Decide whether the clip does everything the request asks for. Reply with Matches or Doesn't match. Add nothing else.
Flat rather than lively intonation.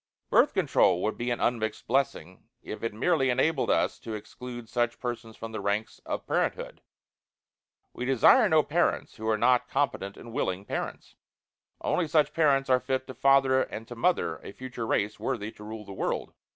Doesn't match